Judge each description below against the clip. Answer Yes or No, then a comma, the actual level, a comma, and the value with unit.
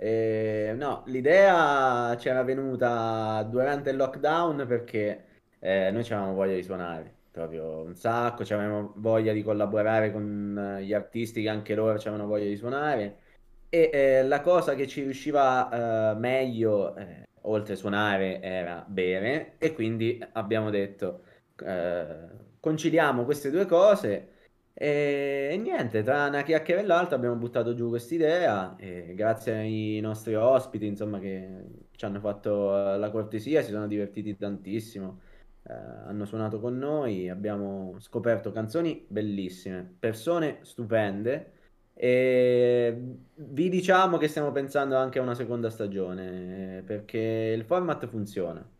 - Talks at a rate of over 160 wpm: No, average, 135 wpm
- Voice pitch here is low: Yes, low, 110 Hz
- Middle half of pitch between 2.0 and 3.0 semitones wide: No, average, 4.2 semitones